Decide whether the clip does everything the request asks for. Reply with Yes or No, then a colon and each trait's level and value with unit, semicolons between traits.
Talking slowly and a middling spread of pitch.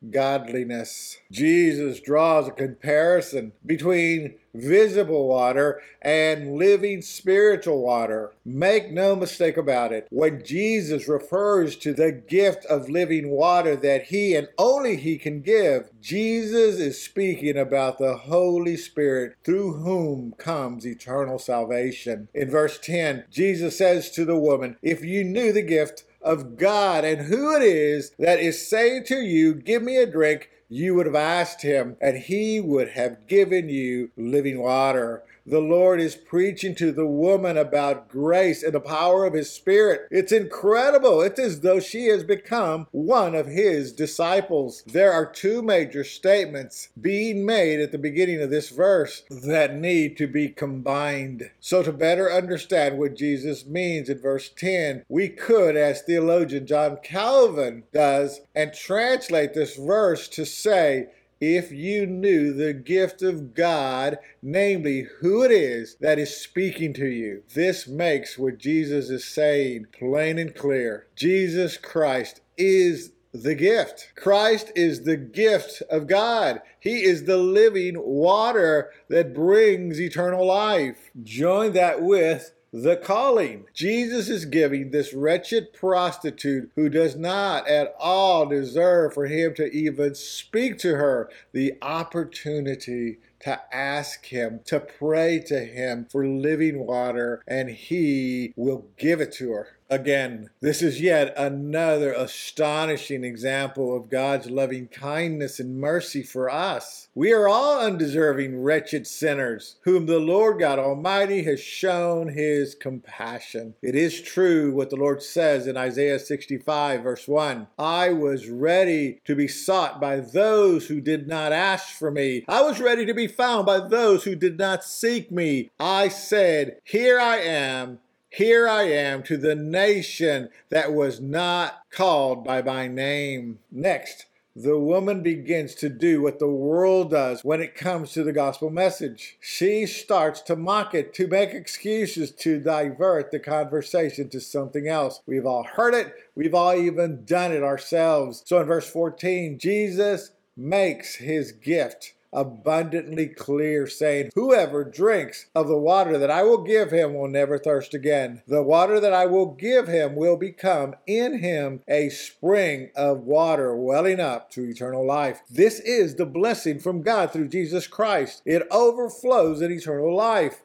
No: average, 150 wpm; average, 4.9 semitones